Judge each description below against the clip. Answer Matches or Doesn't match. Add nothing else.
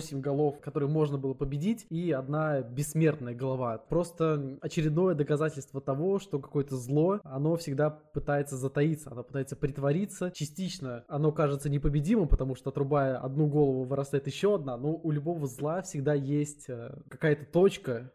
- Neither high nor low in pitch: Matches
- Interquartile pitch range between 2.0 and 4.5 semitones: Matches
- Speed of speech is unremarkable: Matches